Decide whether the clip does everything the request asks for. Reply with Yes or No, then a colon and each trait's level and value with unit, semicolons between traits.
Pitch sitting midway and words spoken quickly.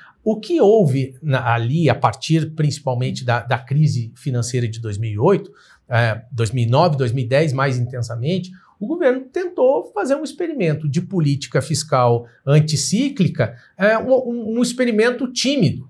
No: medium, 150 Hz; average, 125 wpm